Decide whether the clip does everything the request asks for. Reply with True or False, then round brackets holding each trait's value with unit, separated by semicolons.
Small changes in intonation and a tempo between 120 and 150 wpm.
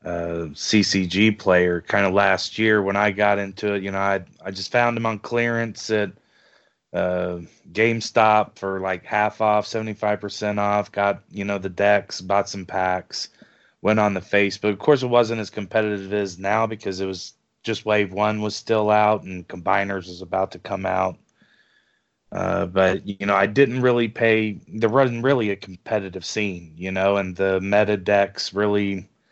False (2.0 semitones; 180 wpm)